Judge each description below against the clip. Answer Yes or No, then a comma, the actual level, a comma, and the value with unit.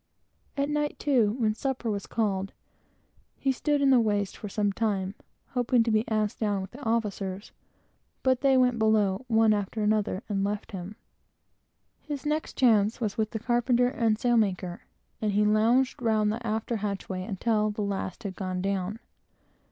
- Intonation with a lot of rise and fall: No, average, 3.0 semitones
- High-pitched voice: Yes, high, 215 Hz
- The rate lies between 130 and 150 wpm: No, average, 170 wpm